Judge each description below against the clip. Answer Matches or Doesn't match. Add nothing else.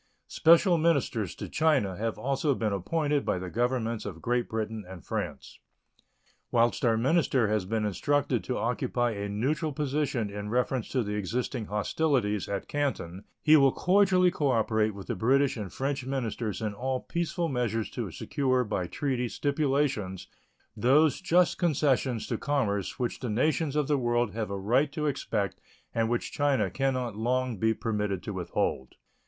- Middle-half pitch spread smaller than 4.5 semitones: Doesn't match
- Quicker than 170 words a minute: Doesn't match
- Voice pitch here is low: Matches